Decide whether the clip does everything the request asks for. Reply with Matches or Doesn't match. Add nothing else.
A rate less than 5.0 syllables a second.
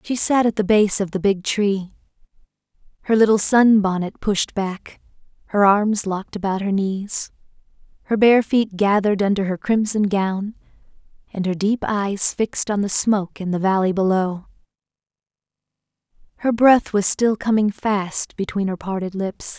Matches